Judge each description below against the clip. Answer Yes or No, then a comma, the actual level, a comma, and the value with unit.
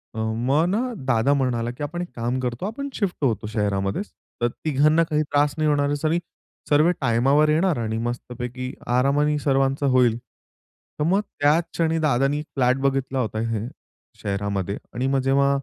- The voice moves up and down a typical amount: Yes, average, 4.0 semitones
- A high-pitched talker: No, low, 135 Hz